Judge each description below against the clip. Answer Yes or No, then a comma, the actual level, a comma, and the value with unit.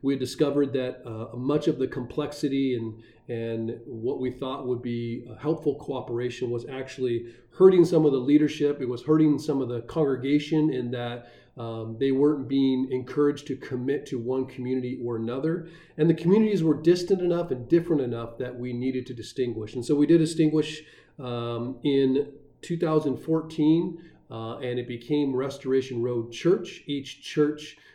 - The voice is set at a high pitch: No, low, 135 Hz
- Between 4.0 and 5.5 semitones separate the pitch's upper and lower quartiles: No, average, 3.6 semitones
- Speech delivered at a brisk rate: No, average, 165 wpm